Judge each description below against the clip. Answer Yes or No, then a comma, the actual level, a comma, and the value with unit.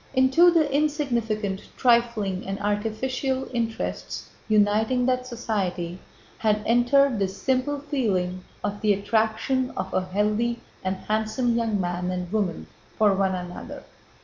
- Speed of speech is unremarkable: No, slow, 125 wpm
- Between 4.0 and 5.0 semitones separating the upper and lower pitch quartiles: Yes, average, 4.5 semitones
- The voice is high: Yes, high, 220 Hz